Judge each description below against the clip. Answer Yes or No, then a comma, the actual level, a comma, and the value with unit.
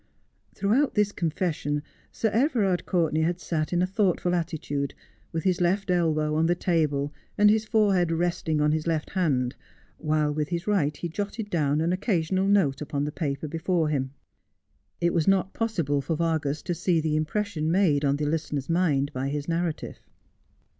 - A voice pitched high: No, medium, 165 Hz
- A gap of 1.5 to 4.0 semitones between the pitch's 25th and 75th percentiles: Yes, average, 3.6 semitones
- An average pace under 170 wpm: No, average, 175 wpm